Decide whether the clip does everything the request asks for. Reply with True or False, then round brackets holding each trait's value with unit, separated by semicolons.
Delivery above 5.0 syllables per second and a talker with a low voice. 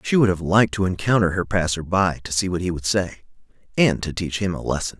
True (6.0 syllables/s; 95 Hz)